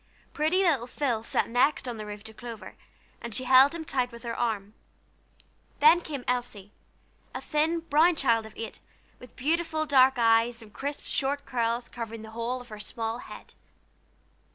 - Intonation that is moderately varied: Yes, average, 4.1 semitones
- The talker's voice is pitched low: No, high, 245 Hz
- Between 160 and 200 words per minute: Yes, average, 175 wpm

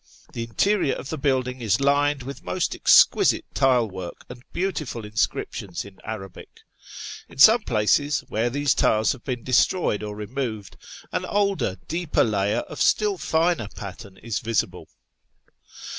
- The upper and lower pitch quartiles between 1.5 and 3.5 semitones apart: No, wide, 5.4 semitones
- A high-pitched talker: No, low, 125 Hz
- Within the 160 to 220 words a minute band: No, average, 145 wpm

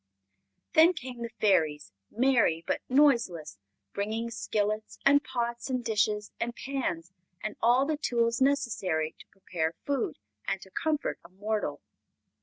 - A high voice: Yes, high, 230 Hz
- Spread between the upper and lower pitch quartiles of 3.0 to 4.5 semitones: No, average, 5.2 semitones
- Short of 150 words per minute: Yes, slow, 135 wpm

